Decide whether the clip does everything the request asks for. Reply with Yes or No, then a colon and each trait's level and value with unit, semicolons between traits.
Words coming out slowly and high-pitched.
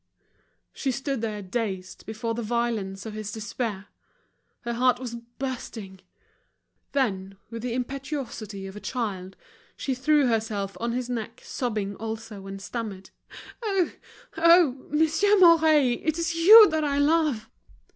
Yes: slow, 130 wpm; high, 235 Hz